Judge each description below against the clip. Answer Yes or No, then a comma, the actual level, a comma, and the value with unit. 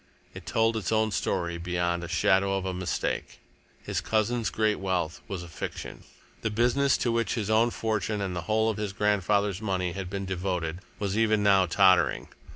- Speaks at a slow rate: No, average, 185 wpm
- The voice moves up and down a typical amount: Yes, average, 3.1 semitones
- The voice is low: Yes, low, 100 Hz